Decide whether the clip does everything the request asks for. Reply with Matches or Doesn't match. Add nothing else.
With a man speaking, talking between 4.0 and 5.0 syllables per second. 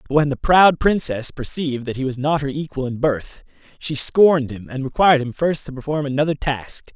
Doesn't match